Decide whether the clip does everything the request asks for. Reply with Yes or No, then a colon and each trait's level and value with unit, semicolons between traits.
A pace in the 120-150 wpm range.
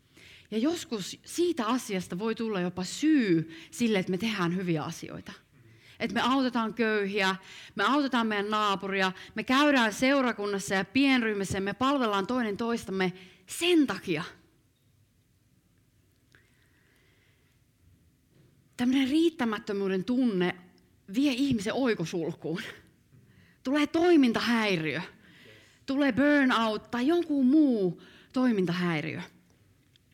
No: slow, 95 wpm